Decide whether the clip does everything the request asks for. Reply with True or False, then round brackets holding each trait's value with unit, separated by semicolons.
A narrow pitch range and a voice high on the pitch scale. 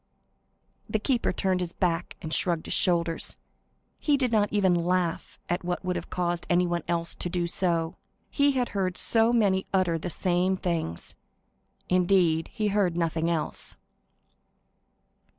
False (2.3 semitones; 180 Hz)